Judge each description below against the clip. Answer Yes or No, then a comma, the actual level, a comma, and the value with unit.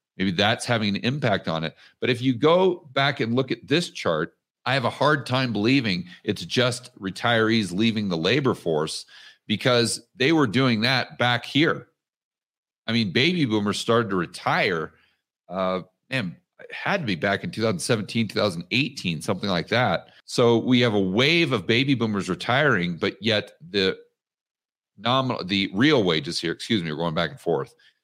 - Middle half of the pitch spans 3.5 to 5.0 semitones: Yes, average, 4.7 semitones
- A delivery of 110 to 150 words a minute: No, average, 175 wpm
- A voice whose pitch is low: Yes, low, 120 Hz